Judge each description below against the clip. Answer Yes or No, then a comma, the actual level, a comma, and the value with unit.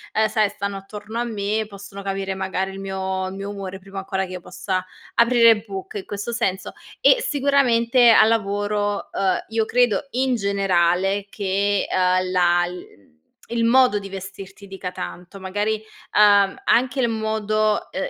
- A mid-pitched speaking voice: No, high, 200 Hz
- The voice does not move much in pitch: Yes, narrow, 2.3 semitones